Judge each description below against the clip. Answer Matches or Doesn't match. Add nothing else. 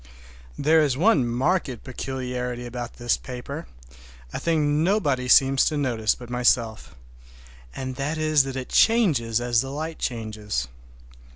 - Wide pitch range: Doesn't match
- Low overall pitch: Matches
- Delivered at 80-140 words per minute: Matches